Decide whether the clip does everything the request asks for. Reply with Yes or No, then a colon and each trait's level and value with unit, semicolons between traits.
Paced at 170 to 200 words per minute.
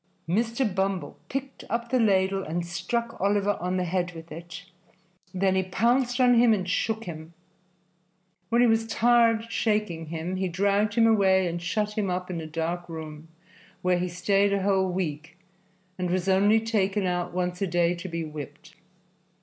Yes: average, 175 wpm